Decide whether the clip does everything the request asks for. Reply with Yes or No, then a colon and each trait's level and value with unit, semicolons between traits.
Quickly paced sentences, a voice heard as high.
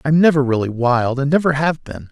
No: fast, 225 wpm; medium, 140 Hz